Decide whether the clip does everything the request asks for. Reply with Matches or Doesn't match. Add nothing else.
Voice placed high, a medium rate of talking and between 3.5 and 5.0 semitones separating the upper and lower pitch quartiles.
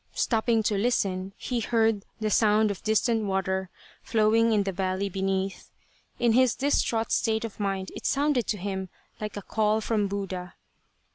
Doesn't match